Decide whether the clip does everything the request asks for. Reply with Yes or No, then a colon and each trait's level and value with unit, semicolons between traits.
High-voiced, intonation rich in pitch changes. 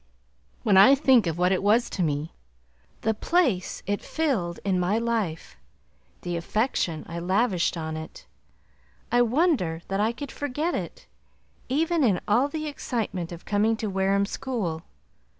Yes: high, 205 Hz; wide, 6.1 semitones